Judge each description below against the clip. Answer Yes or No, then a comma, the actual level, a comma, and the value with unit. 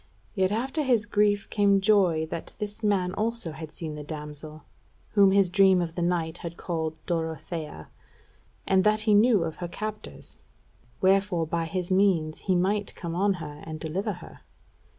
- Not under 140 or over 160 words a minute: No, average, 170 wpm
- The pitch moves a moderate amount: Yes, average, 4.0 semitones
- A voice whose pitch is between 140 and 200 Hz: Yes, medium, 185 Hz